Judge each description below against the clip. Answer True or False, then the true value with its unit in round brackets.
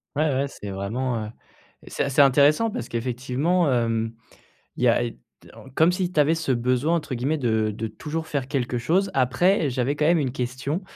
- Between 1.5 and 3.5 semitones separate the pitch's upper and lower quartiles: False (4.4 semitones)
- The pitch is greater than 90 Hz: True (135 Hz)